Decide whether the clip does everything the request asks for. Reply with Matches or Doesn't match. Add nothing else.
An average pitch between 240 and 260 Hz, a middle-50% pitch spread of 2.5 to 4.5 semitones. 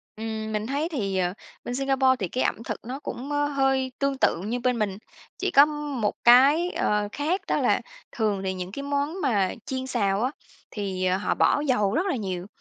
Doesn't match